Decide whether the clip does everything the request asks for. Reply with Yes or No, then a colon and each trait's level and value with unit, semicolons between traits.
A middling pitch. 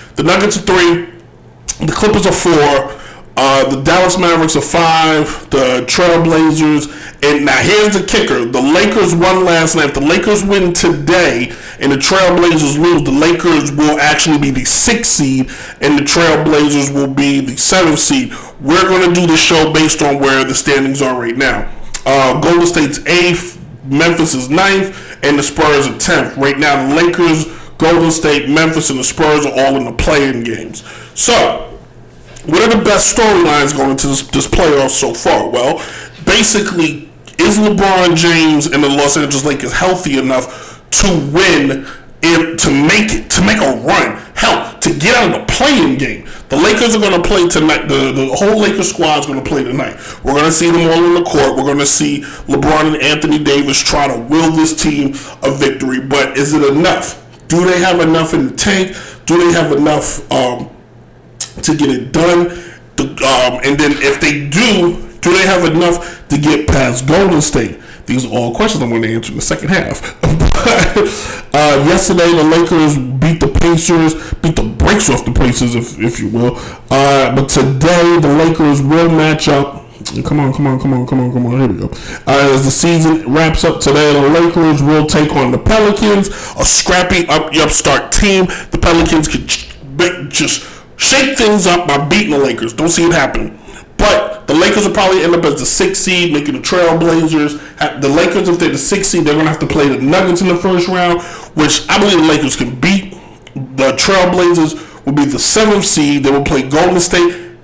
Yes: medium, 155 Hz